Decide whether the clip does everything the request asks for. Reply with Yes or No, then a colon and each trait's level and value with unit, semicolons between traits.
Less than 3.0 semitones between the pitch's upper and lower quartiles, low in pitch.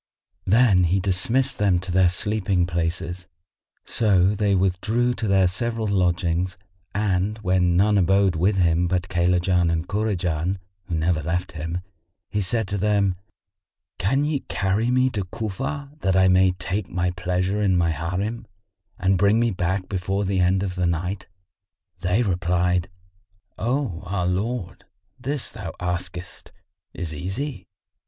Yes: narrow, 2.6 semitones; very low, 95 Hz